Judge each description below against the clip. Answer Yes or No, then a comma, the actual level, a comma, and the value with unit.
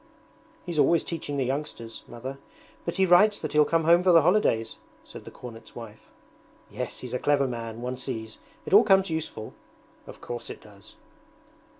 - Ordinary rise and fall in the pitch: No, wide, 6.4 semitones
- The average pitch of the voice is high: No, medium, 140 Hz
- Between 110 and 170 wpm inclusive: No, average, 180 wpm